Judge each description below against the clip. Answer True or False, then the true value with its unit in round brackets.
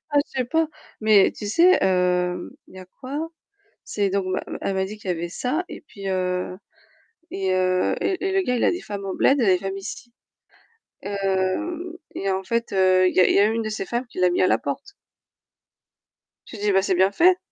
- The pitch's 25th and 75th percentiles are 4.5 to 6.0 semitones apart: True (5.0 semitones)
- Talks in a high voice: True (195 Hz)